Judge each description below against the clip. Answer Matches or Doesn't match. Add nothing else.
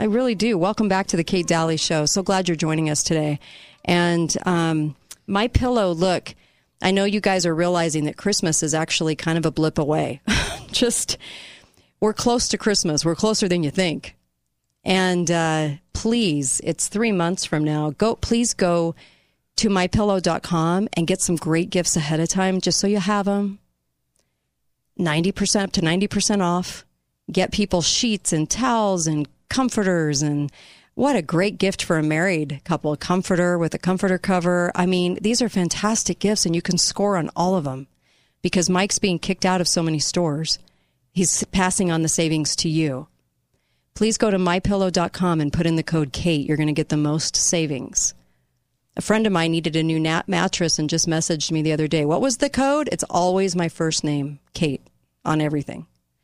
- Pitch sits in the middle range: Matches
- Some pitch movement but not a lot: Matches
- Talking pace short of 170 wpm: Doesn't match